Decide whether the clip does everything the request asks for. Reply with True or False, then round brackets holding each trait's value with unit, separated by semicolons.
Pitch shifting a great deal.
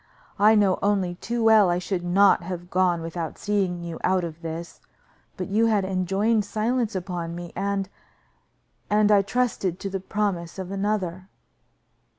False (2.8 semitones)